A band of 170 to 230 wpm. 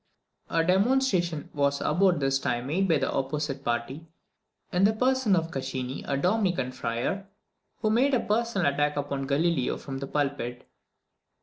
No: average, 150 wpm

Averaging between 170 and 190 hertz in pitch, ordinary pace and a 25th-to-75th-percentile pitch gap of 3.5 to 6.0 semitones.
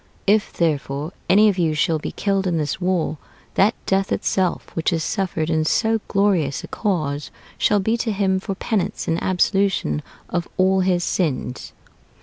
Yes: medium, 185 Hz; average, 165 wpm; average, 3.8 semitones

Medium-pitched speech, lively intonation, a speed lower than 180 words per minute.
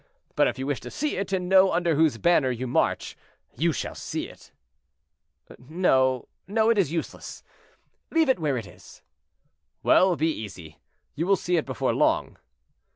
Yes: medium, 160 Hz; wide, 6.3 semitones; average, 170 wpm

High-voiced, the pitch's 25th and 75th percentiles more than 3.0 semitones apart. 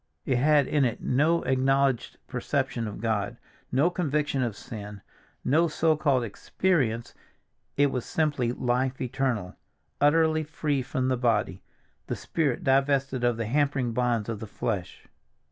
No: low, 130 Hz; average, 3.7 semitones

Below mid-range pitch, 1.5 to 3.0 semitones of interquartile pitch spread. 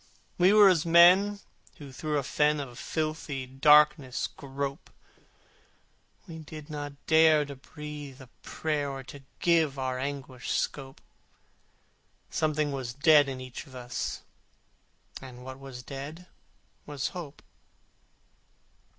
No: medium, 145 Hz; narrow, 2.6 semitones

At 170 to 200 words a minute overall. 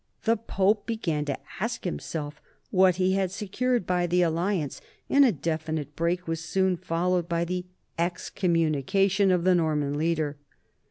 No: average, 150 wpm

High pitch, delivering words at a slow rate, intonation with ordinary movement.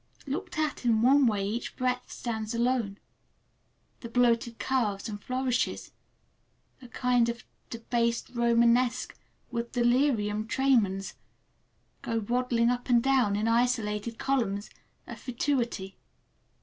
No: high, 235 Hz; slow, 110 wpm; narrow, 2.1 semitones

